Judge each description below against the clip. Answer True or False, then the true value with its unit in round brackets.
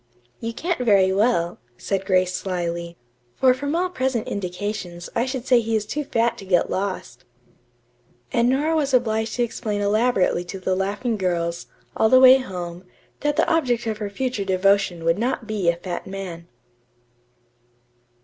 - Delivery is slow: False (170 wpm)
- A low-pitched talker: False (205 Hz)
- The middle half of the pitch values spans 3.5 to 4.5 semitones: False (5.1 semitones)